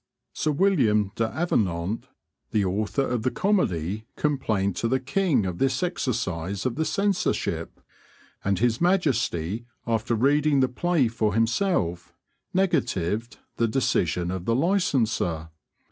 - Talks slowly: Yes, slow, 125 wpm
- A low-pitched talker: Yes, low, 115 Hz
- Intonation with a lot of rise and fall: Yes, wide, 6.7 semitones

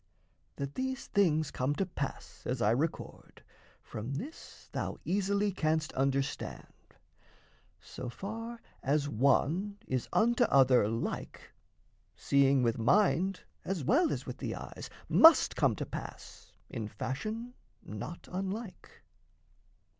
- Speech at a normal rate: No, slow, 120 wpm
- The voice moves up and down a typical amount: No, wide, 7.4 semitones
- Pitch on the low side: No, medium, 155 Hz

